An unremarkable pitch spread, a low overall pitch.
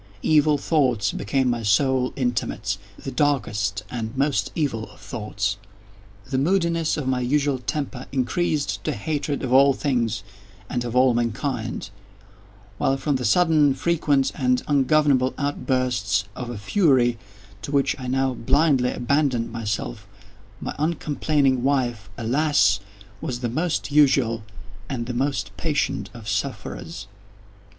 Yes: average, 3.5 semitones; low, 130 Hz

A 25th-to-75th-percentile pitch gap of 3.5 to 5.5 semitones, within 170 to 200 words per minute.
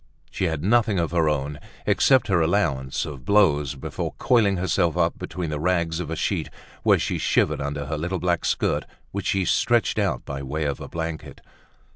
Yes: average, 3.9 semitones; average, 190 wpm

